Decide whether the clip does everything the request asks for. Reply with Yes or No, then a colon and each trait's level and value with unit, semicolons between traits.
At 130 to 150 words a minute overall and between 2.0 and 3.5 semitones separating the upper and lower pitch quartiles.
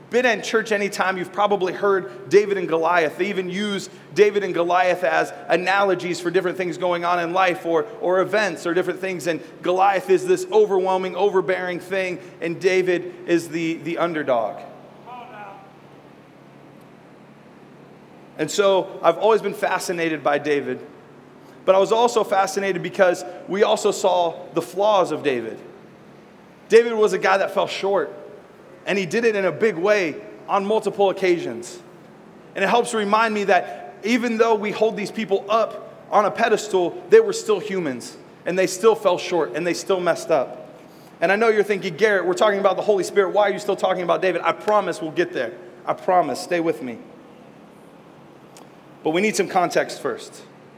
No: average, 175 wpm; average, 2.9 semitones